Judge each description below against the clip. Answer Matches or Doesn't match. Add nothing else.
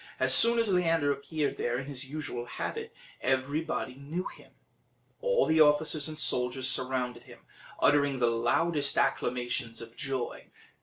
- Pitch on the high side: Doesn't match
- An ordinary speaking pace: Matches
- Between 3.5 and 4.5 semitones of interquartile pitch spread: Matches